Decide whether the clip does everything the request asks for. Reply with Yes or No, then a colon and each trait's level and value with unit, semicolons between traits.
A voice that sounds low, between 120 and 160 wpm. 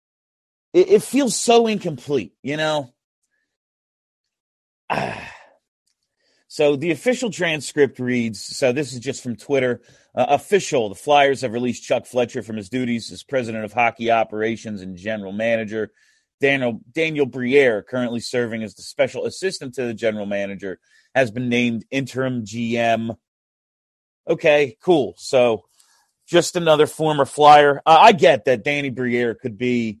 Yes: low, 125 Hz; average, 140 wpm